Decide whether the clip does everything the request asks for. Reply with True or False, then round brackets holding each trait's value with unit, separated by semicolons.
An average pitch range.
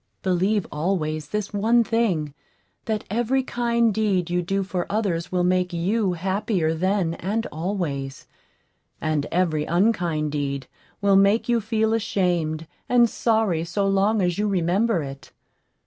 True (4.6 semitones)